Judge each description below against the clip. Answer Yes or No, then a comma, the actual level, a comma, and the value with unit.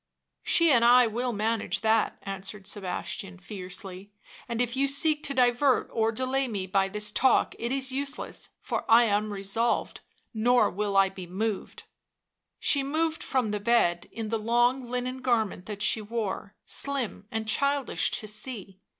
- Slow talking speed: No, average, 165 wpm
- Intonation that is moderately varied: Yes, average, 4.0 semitones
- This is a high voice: Yes, high, 225 Hz